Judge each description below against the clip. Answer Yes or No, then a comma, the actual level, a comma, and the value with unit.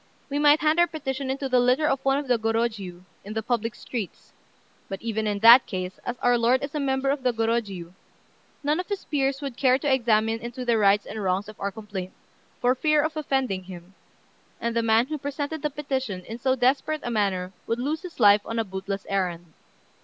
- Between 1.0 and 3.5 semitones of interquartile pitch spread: No, average, 4.8 semitones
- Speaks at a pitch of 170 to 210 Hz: No, high, 240 Hz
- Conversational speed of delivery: No, fast, 215 wpm